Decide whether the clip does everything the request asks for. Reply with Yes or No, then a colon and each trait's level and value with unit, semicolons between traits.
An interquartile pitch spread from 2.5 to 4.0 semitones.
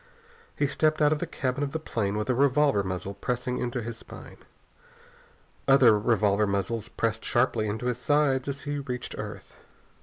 No: average, 4.6 semitones